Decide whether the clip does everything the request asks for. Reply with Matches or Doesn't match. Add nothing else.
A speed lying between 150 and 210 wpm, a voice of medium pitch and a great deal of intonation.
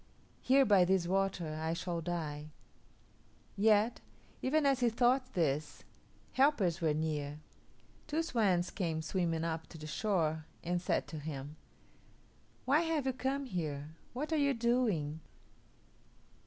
Doesn't match